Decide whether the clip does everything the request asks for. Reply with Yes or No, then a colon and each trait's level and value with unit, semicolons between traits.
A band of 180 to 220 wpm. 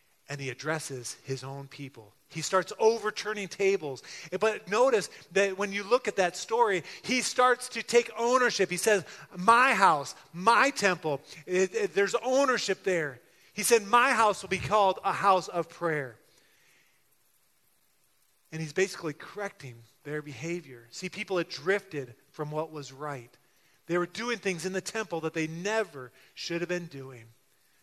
No: average, 160 wpm